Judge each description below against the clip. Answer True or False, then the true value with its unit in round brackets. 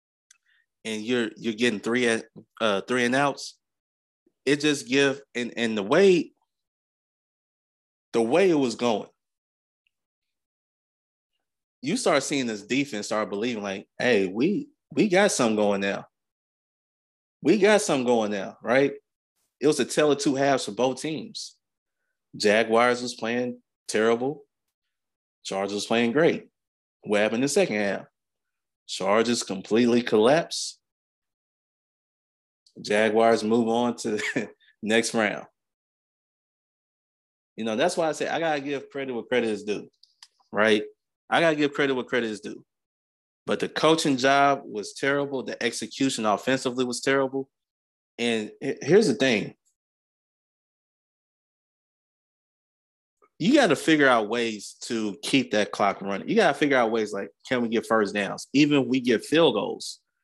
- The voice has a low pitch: True (120 Hz)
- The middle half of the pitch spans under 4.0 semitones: False (4.4 semitones)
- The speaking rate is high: False (145 wpm)